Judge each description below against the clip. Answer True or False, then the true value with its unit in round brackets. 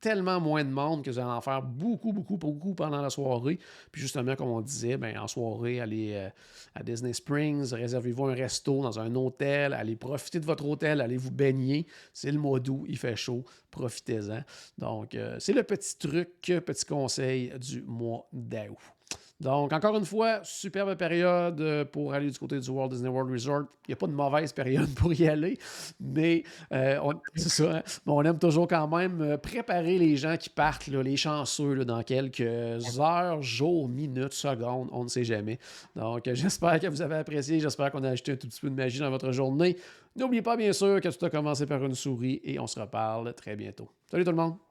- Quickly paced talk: False (205 wpm)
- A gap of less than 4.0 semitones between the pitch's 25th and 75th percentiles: False (4.3 semitones)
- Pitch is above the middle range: False (140 Hz)